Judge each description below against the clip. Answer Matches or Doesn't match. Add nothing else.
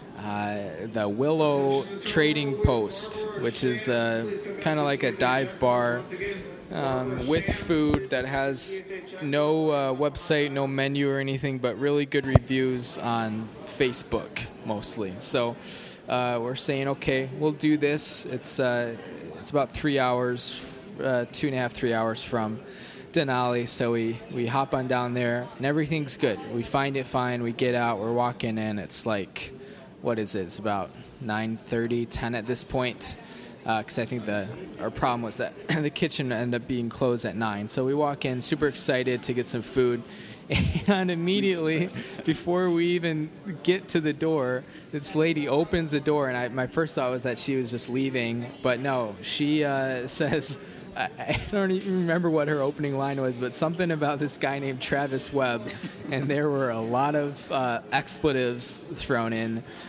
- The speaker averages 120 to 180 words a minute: Matches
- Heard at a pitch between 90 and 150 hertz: Matches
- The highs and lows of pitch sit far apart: Doesn't match